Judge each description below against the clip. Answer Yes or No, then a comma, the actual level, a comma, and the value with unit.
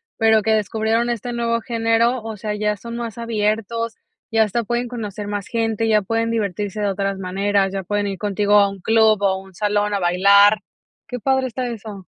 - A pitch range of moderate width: No, narrow, 2.2 semitones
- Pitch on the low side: No, high, 215 Hz